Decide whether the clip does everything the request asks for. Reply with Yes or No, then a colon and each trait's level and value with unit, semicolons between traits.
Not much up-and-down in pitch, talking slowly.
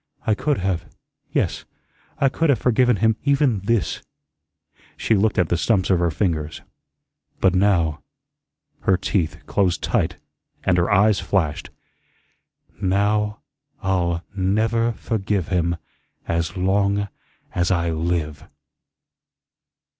No: average, 3.7 semitones; slow, 115 wpm